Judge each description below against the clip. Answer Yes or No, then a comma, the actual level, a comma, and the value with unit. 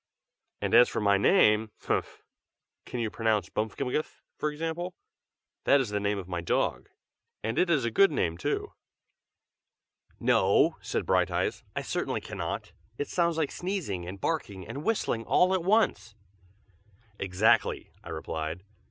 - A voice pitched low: Yes, low, 115 Hz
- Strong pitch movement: Yes, wide, 8.6 semitones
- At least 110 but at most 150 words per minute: Yes, average, 145 wpm